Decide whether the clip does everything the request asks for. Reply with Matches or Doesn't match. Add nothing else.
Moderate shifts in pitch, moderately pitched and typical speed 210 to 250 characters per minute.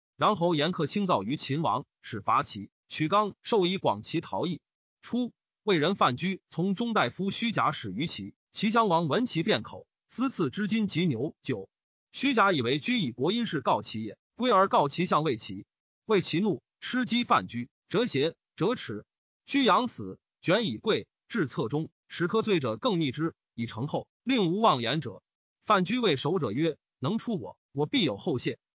Doesn't match